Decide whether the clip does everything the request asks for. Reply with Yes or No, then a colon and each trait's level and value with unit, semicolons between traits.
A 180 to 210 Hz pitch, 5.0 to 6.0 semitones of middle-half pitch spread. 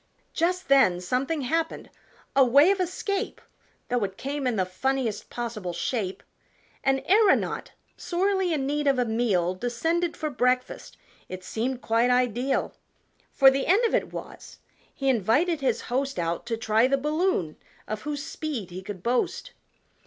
No: very high, 260 Hz; wide, 5.4 semitones